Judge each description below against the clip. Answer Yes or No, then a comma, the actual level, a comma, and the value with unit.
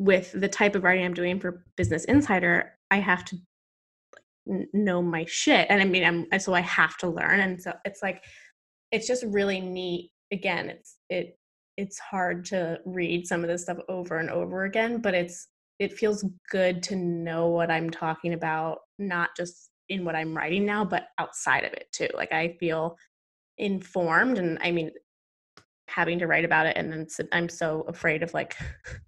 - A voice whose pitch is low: No, medium, 180 Hz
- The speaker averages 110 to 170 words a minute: No, average, 185 wpm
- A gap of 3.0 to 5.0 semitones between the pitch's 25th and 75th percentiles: No, narrow, 2.6 semitones